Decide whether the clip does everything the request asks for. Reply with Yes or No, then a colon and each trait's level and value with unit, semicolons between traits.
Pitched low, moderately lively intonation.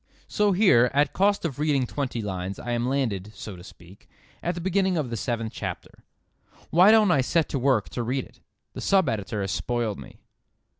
No: low, 130 Hz; wide, 7.7 semitones